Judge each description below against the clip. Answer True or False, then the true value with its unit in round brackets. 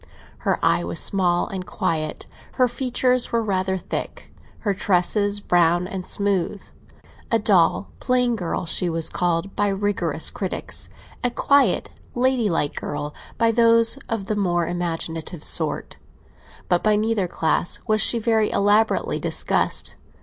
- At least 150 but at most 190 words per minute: False (135 wpm)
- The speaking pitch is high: True (195 Hz)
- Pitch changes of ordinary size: True (4.4 semitones)